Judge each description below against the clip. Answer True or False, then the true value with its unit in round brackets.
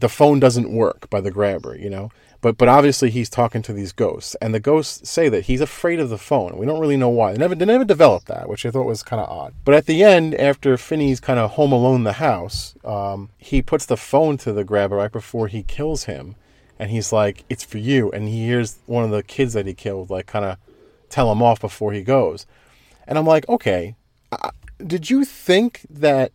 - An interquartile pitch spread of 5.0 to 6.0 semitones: True (5.5 semitones)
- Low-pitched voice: True (120 Hz)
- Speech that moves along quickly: True (245 wpm)